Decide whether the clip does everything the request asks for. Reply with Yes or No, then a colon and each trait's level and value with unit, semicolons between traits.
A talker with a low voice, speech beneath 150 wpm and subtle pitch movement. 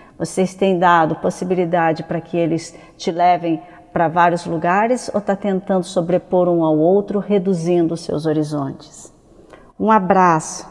No: medium, 175 Hz; average, 140 wpm; narrow, 2.2 semitones